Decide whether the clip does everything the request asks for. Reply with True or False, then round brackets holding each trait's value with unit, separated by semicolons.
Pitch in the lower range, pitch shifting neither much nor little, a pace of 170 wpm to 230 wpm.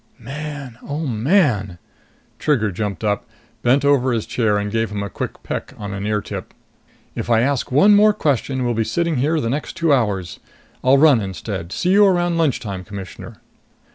False (125 Hz; 6.3 semitones; 180 wpm)